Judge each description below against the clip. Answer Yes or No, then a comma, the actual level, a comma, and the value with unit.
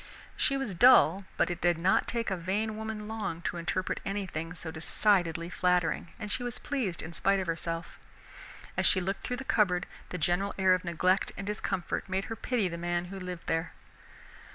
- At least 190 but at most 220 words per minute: Yes, average, 195 wpm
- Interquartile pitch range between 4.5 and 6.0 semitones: No, average, 3.4 semitones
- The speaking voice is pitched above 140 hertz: Yes, medium, 185 Hz